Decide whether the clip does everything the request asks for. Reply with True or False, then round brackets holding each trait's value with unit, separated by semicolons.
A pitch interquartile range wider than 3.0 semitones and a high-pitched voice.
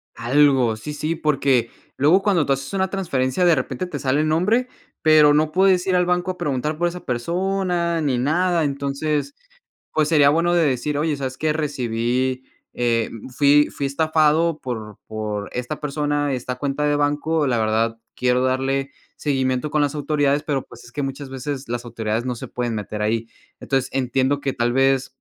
False (3.7 semitones; 140 Hz)